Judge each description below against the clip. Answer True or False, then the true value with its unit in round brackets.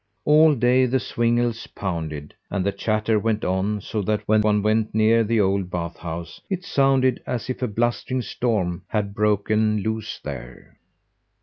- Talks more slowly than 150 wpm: False (165 wpm)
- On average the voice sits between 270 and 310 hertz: False (110 Hz)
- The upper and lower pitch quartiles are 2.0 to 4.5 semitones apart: True (3.2 semitones)